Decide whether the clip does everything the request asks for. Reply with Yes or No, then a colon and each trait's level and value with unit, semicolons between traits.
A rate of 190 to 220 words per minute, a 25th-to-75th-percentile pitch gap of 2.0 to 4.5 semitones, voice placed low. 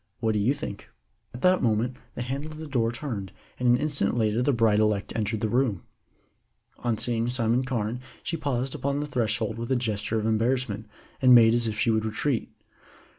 Yes: average, 200 wpm; average, 2.8 semitones; low, 120 Hz